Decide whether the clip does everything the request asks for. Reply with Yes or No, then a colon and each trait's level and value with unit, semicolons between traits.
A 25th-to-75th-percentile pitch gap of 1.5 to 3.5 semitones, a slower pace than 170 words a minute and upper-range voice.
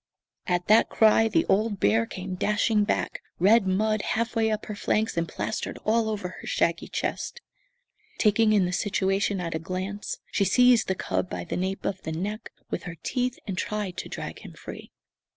No: average, 3.0 semitones; average, 190 wpm; high, 205 Hz